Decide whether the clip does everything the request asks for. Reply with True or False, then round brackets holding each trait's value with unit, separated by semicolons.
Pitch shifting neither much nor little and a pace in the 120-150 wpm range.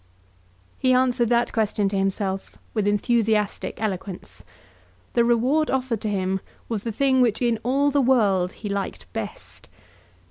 True (3.9 semitones; 145 wpm)